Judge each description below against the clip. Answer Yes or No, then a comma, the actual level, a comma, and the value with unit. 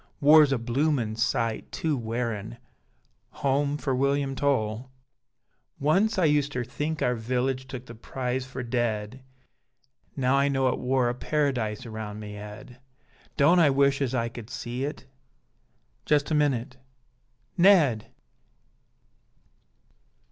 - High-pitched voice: No, low, 130 Hz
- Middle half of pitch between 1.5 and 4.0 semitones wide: Yes, average, 3.4 semitones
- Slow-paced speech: Yes, slow, 130 wpm